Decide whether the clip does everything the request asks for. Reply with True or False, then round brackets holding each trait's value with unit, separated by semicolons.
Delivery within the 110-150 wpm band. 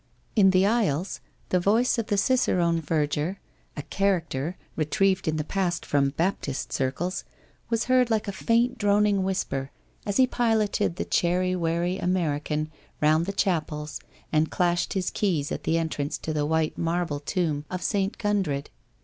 False (160 wpm)